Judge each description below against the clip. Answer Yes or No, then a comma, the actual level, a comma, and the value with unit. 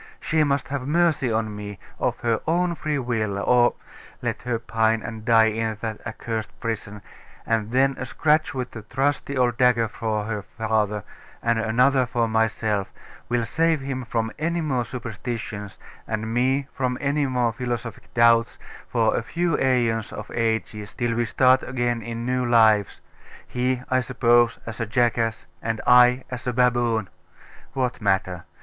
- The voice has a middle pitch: No, low, 120 Hz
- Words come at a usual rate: Yes, average, 160 wpm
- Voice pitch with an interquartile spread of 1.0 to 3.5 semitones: Yes, narrow, 2.4 semitones